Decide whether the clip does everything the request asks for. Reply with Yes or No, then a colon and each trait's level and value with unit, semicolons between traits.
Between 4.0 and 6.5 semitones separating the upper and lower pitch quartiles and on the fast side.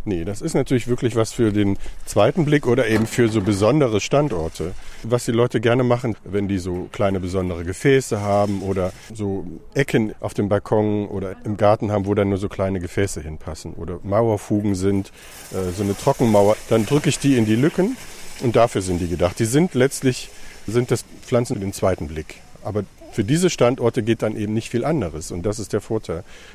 No: average, 3.6 semitones; fast, 195 wpm